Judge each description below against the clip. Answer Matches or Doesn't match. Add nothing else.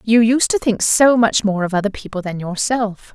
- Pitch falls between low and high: Doesn't match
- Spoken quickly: Matches